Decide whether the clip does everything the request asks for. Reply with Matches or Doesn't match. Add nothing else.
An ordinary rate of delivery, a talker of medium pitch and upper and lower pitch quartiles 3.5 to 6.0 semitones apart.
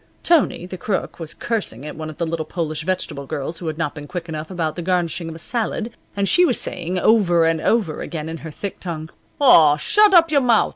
Doesn't match